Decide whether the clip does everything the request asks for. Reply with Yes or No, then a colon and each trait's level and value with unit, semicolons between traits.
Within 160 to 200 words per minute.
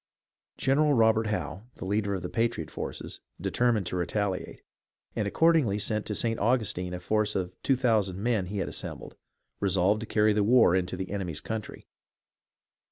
Yes: average, 165 wpm